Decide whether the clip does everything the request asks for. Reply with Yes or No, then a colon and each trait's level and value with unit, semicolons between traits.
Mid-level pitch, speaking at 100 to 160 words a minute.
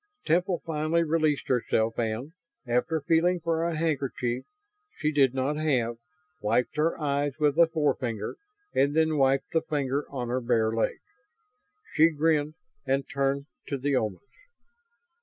Yes: medium, 145 Hz; average, 140 wpm